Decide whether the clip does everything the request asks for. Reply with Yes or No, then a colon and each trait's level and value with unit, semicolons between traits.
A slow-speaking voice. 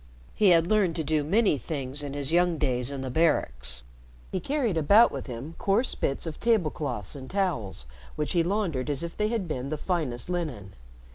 No: average, 195 wpm